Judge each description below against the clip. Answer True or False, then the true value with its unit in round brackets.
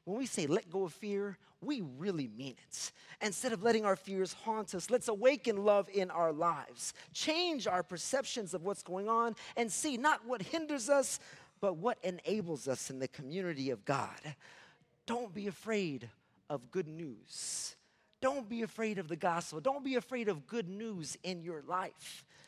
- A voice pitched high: True (200 Hz)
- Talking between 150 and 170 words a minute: False (180 wpm)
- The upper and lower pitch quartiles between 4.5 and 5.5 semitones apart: True (5.1 semitones)